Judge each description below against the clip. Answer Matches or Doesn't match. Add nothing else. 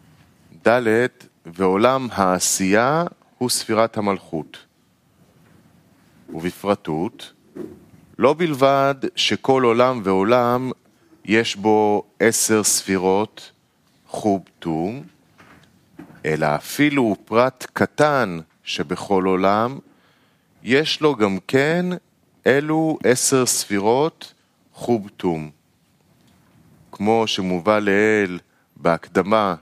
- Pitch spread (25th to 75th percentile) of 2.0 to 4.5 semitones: Doesn't match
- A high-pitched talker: Doesn't match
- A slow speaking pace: Matches